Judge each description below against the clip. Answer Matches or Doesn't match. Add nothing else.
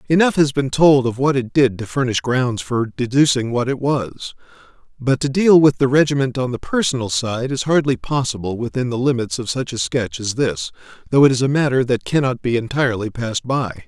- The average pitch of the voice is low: Matches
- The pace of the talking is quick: Matches